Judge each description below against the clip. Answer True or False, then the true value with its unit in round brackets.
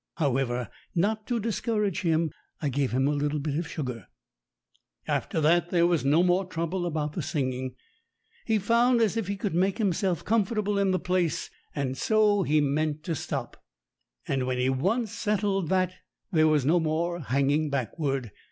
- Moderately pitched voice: True (165 Hz)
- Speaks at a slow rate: False (170 wpm)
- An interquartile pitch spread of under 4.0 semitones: False (5.5 semitones)